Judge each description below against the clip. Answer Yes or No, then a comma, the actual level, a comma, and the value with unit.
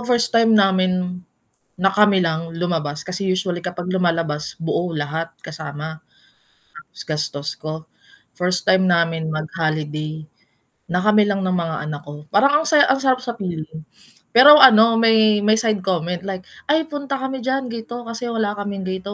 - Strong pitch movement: Yes, wide, 5.9 semitones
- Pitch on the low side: No, medium, 185 Hz